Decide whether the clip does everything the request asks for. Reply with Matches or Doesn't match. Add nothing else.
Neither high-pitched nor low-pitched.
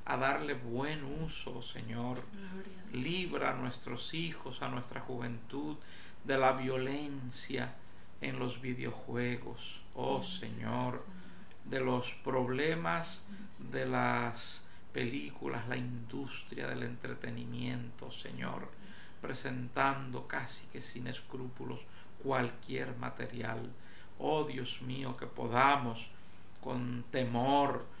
Doesn't match